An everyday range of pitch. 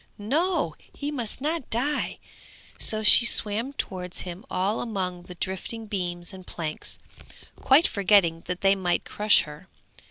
Yes: average, 4.5 semitones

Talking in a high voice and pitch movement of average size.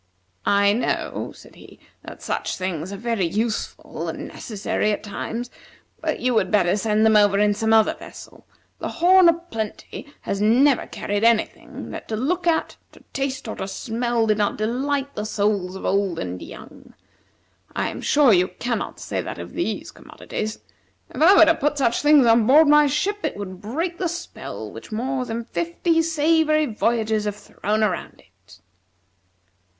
No: high, 225 Hz; wide, 5.7 semitones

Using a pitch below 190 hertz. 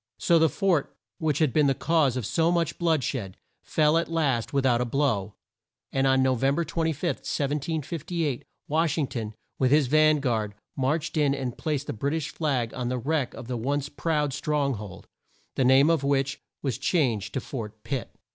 Yes: medium, 140 Hz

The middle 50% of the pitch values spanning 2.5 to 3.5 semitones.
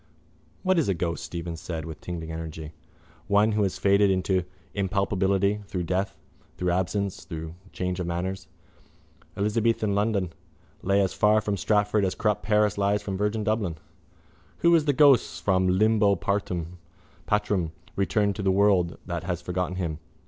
Yes: average, 2.8 semitones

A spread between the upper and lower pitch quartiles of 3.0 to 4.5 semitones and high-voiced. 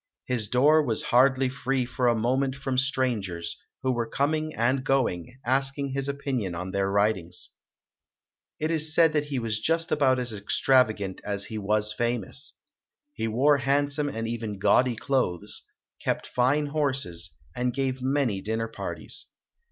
No: average, 4.1 semitones; low, 125 Hz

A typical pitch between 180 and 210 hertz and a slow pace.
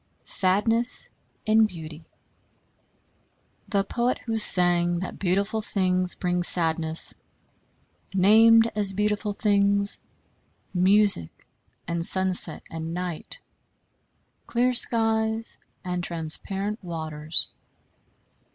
Yes: high, 190 Hz; slow, 85 wpm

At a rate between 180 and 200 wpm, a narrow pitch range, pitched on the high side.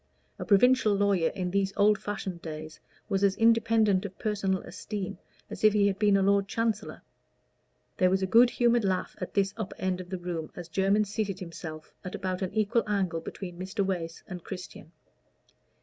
Yes: average, 185 wpm; narrow, 2.3 semitones; high, 195 Hz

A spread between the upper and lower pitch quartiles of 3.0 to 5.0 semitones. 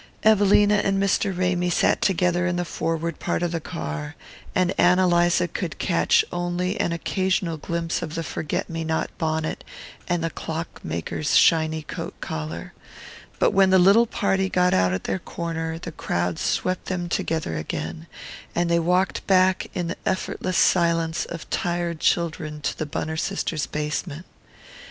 No: narrow, 2.4 semitones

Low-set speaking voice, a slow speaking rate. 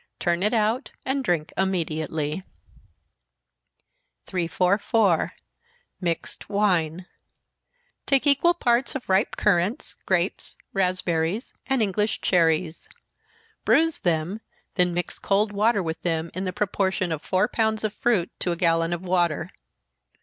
No: medium, 185 Hz; slow, 120 wpm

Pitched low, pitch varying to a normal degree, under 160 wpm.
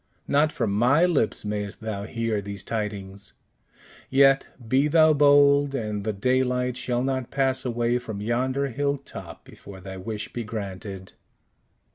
Yes: low, 120 Hz; average, 4.7 semitones; average, 145 wpm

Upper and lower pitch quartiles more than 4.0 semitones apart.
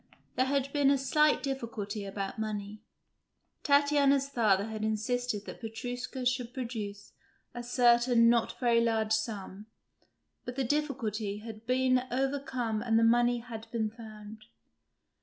No: average, 2.9 semitones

